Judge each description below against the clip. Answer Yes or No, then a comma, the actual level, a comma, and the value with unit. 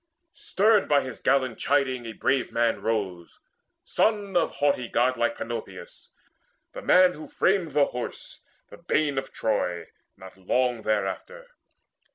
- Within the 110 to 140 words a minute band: Yes, slow, 135 wpm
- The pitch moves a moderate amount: No, wide, 8.1 semitones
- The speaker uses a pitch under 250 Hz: Yes, low, 135 Hz